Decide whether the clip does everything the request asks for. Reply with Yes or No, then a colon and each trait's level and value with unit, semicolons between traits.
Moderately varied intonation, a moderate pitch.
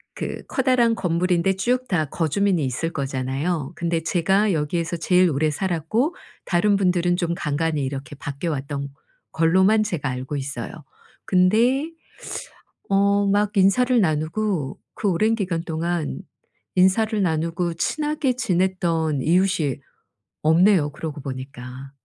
Yes: average, 4.7 semitones; medium, 175 Hz